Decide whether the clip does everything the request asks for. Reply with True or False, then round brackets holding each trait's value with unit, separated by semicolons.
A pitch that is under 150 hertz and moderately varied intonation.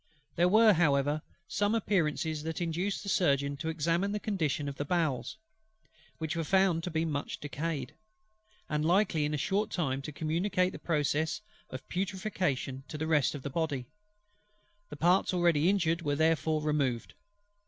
False (160 Hz; 3.6 semitones)